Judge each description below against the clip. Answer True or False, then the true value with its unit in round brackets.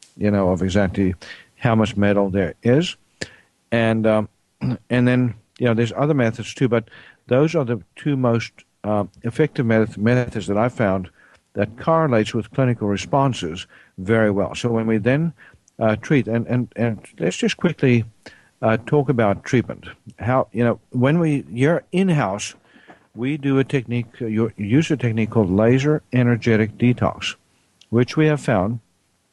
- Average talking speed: True (160 wpm)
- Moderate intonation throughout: True (4.0 semitones)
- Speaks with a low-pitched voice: True (115 Hz)